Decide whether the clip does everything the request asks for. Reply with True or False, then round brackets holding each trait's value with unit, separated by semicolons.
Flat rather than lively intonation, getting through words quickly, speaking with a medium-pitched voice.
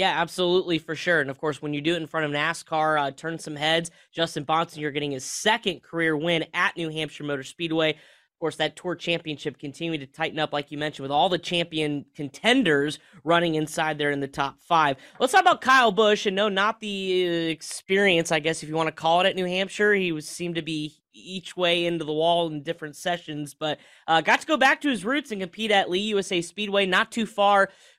False (3.6 semitones; 230 wpm; 165 Hz)